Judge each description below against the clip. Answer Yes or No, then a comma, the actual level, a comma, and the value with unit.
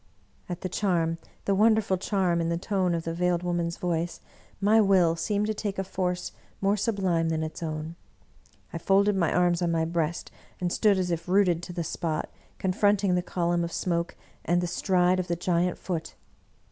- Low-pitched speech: No, medium, 180 Hz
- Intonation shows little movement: Yes, narrow, 2.3 semitones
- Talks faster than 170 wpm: Yes, average, 195 wpm